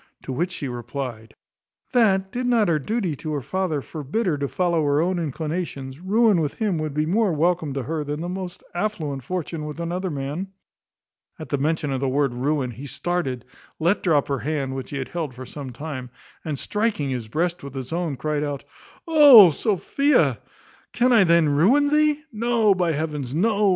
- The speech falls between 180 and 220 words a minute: Yes, average, 190 wpm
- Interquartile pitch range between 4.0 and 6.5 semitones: Yes, average, 5.1 semitones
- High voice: No, medium, 160 Hz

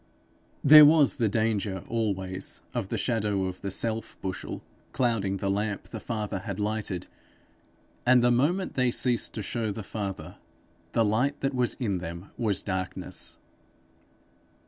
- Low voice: Yes, low, 110 Hz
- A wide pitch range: No, average, 3.8 semitones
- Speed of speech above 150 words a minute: No, average, 145 wpm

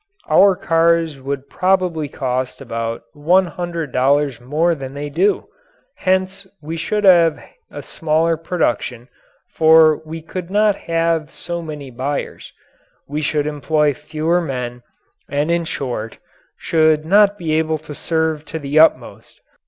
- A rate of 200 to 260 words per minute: No, slow, 135 wpm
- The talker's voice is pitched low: No, medium, 155 Hz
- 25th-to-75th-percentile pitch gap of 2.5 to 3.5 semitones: Yes, average, 2.9 semitones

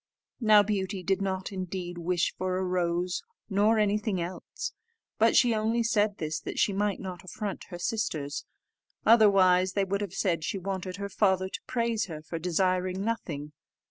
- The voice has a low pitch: No, high, 190 Hz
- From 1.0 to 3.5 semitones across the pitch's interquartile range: Yes, narrow, 2.4 semitones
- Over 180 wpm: No, average, 170 wpm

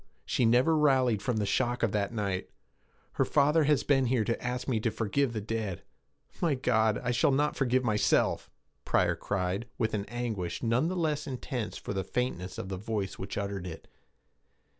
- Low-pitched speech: Yes, low, 115 Hz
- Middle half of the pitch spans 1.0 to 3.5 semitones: No, average, 4.2 semitones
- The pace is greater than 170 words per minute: Yes, average, 185 wpm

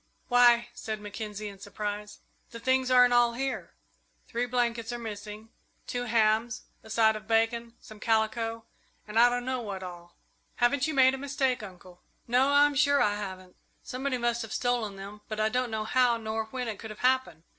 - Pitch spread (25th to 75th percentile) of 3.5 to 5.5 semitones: No, narrow, 2.6 semitones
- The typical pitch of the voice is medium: No, high, 230 Hz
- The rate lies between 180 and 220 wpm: Yes, average, 190 wpm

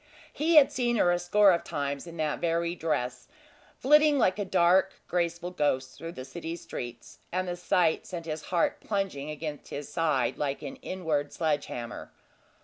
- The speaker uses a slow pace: No, average, 175 wpm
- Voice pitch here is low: No, medium, 170 Hz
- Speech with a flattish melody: No, average, 4.1 semitones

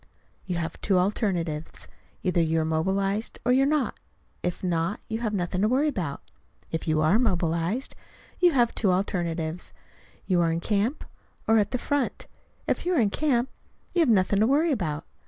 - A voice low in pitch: No, high, 195 Hz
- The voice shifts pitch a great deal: Yes, wide, 6.1 semitones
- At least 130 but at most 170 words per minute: No, average, 185 wpm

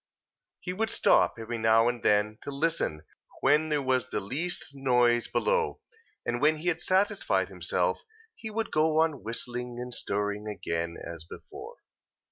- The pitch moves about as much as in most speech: No, wide, 6.5 semitones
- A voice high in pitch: No, low, 130 Hz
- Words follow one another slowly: No, average, 155 wpm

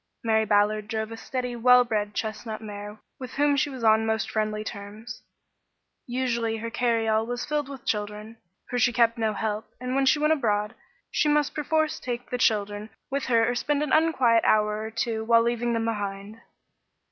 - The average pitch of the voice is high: Yes, high, 230 Hz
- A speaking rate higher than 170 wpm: Yes, average, 185 wpm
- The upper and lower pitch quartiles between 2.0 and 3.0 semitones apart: Yes, narrow, 2.6 semitones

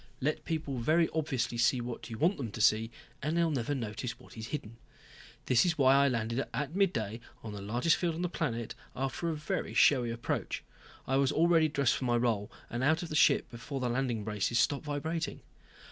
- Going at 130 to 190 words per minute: No, fast, 205 wpm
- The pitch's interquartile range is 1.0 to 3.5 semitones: No, average, 5.0 semitones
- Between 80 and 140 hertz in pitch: Yes, low, 135 Hz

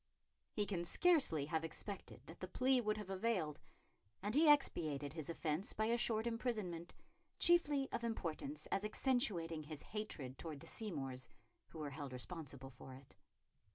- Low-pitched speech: No, medium, 180 Hz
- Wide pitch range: Yes, wide, 7.1 semitones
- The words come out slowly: No, average, 155 wpm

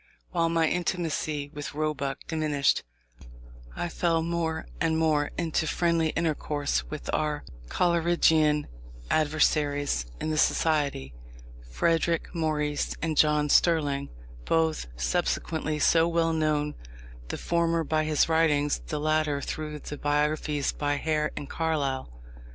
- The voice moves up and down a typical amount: No, narrow, 1.8 semitones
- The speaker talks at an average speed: No, slow, 120 wpm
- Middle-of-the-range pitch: Yes, medium, 155 Hz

